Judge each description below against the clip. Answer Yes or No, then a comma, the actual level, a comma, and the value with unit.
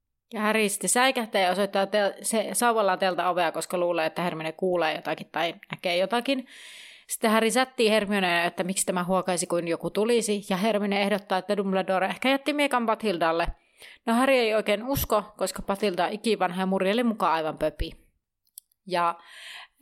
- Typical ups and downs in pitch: Yes, average, 3.8 semitones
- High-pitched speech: Yes, high, 195 Hz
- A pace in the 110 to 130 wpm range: No, fast, 155 wpm